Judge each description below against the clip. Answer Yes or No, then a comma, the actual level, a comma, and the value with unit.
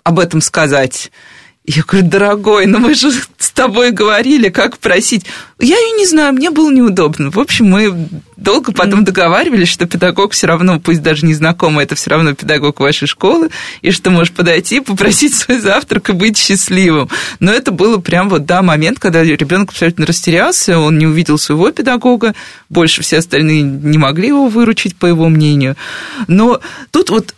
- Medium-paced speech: No, fast, 175 wpm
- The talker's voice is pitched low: No, medium, 185 Hz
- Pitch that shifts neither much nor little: No, wide, 6.0 semitones